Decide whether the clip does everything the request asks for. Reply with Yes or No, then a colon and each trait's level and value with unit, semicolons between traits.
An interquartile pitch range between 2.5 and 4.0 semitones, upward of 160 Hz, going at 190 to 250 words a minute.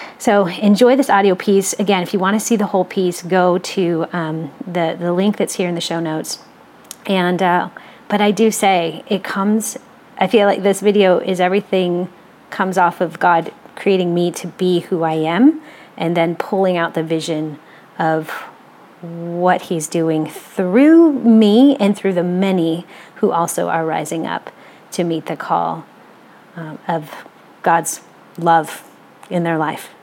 No: average, 3.1 semitones; medium, 185 Hz; average, 170 wpm